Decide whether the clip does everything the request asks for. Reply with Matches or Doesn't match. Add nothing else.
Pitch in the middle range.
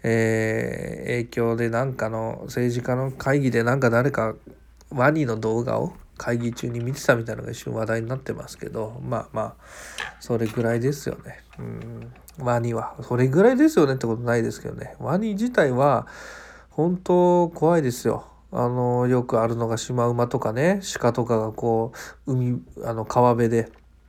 Doesn't match